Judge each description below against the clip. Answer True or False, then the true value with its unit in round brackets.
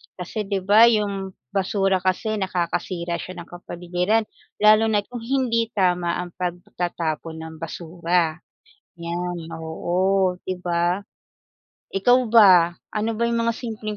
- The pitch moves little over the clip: False (3.5 semitones)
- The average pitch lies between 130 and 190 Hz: True (185 Hz)